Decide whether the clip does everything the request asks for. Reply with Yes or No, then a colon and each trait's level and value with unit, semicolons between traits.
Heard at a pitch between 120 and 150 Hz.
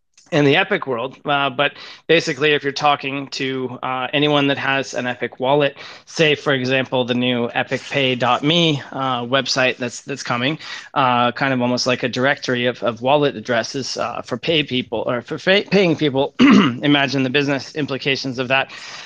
Yes: low, 135 Hz